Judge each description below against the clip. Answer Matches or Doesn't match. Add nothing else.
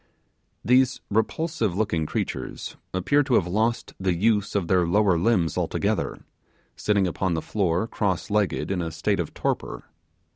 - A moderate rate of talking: Matches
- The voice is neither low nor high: Doesn't match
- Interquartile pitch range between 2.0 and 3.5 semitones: Doesn't match